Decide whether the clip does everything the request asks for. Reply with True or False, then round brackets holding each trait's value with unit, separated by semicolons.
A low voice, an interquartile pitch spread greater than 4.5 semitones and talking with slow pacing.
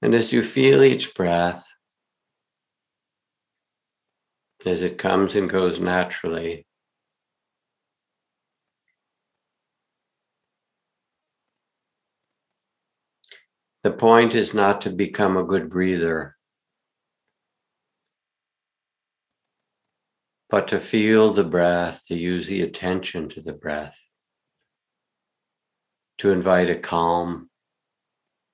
False (90 Hz; 2.7 semitones; 80 wpm)